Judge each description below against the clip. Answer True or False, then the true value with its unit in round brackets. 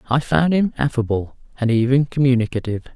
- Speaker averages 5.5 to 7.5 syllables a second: True (6.1 syllables/s)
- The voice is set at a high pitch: False (125 Hz)